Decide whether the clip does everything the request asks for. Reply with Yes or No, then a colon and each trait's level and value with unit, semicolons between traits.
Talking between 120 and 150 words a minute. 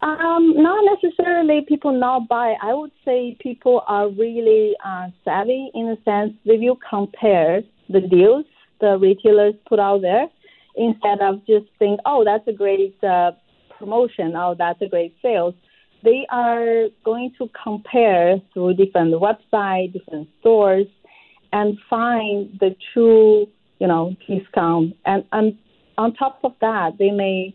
Yes: average, 145 wpm